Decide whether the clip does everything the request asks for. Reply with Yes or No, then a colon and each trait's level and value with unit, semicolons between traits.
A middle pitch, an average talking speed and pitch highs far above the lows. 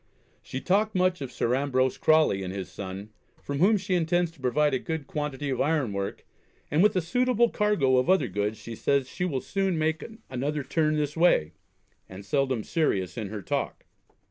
Yes: medium, 145 Hz; average, 195 wpm; wide, 6.1 semitones